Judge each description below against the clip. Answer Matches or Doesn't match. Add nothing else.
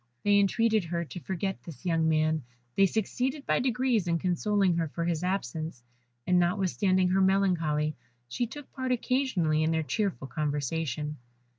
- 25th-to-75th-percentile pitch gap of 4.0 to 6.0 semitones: Matches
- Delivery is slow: Doesn't match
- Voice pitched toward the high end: Doesn't match